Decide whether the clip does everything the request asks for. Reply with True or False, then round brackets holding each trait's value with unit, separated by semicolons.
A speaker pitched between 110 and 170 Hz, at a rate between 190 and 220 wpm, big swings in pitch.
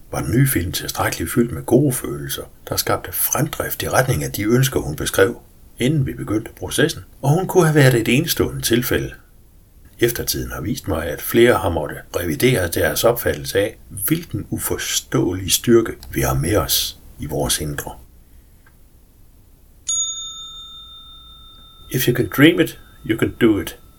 False (135 Hz; 160 wpm; 8.3 semitones)